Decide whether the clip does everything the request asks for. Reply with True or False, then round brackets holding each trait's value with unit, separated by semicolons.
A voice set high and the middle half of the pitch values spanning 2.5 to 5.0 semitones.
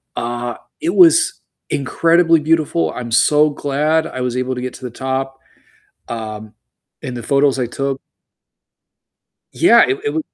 False (135 Hz; 4.2 semitones)